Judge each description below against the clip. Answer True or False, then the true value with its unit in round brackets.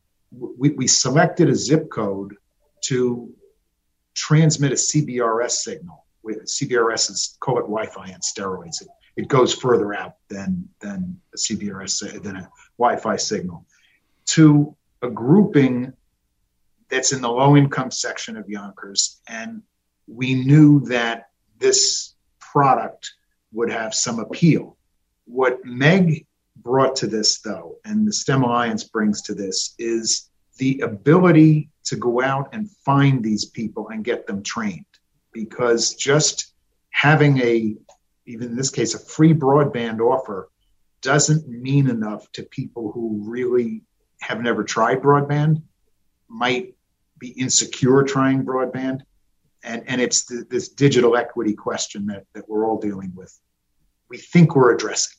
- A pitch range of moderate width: True (5.0 semitones)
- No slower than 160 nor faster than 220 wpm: False (135 wpm)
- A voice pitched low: True (130 Hz)